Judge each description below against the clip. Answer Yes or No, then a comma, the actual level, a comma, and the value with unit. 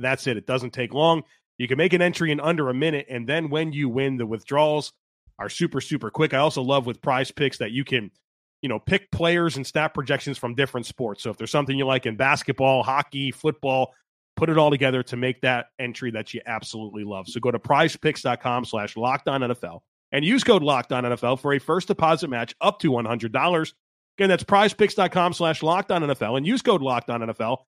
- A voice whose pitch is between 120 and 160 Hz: Yes, low, 135 Hz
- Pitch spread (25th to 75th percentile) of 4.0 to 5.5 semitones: Yes, average, 4.3 semitones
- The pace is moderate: No, fast, 210 wpm